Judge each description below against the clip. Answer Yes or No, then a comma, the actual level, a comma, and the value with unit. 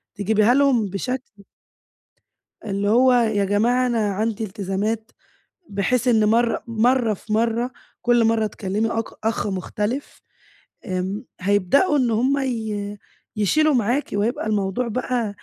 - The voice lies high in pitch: Yes, high, 220 Hz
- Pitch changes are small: No, average, 3.1 semitones